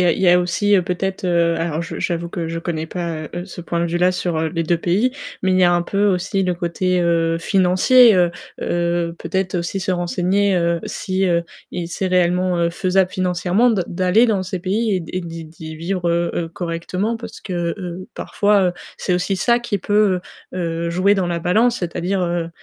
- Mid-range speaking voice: Yes, medium, 180 Hz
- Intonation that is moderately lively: No, narrow, 1.9 semitones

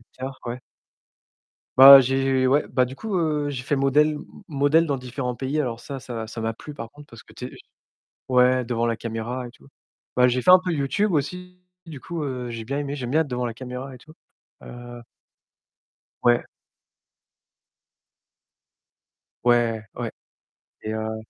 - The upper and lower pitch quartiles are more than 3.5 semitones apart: No, average, 3.2 semitones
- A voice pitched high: No, low, 130 Hz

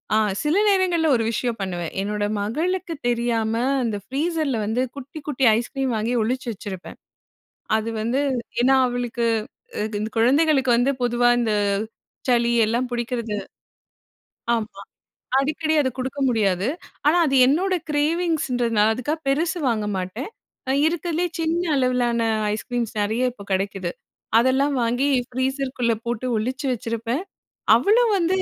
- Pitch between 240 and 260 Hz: Yes, high, 245 Hz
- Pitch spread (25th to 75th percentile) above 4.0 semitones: Yes, average, 4.4 semitones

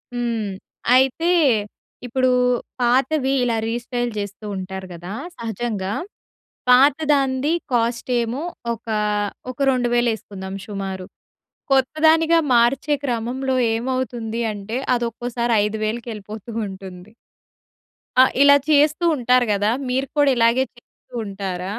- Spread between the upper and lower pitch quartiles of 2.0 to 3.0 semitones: No, average, 3.7 semitones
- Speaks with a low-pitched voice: No, high, 240 Hz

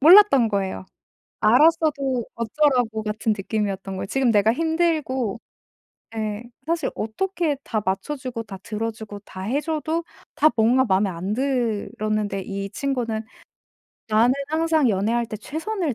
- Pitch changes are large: Yes, wide, 5.8 semitones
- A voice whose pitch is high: Yes, high, 230 Hz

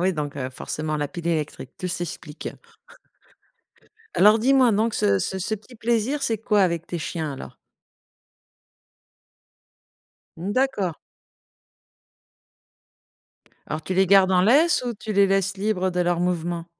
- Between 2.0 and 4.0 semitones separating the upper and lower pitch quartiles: No, average, 4.5 semitones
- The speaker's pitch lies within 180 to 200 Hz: Yes, medium, 185 Hz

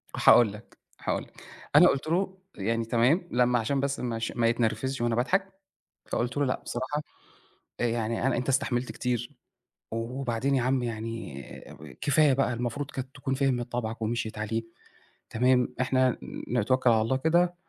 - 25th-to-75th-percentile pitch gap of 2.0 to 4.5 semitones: Yes, average, 2.8 semitones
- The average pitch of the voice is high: No, low, 125 Hz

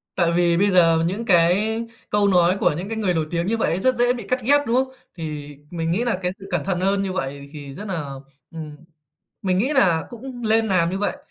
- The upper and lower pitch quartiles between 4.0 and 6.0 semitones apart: Yes, average, 4.8 semitones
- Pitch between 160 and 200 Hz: Yes, medium, 185 Hz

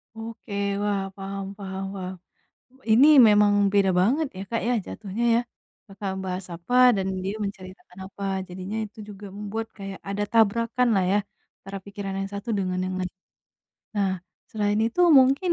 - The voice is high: Yes, high, 200 Hz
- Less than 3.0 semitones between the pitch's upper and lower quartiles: Yes, narrow, 2.6 semitones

